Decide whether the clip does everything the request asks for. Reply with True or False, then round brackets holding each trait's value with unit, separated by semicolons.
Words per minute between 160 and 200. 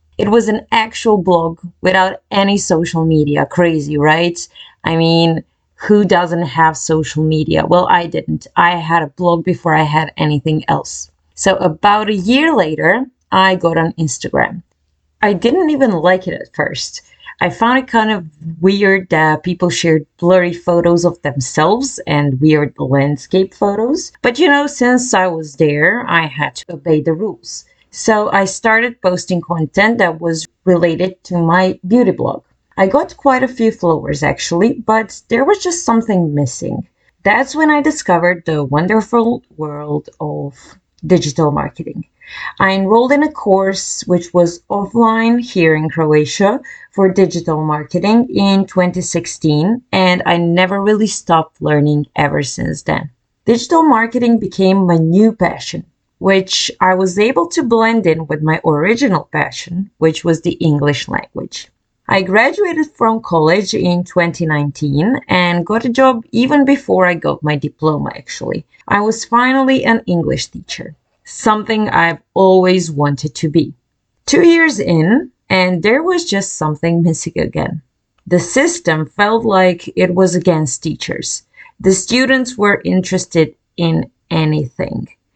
False (150 wpm)